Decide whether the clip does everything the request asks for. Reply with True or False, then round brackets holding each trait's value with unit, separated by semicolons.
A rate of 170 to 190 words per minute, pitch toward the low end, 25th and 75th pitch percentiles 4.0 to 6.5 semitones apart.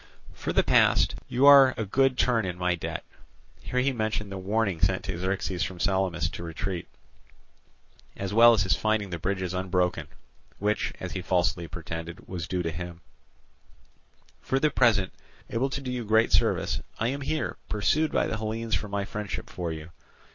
True (175 wpm; 100 Hz; 4.3 semitones)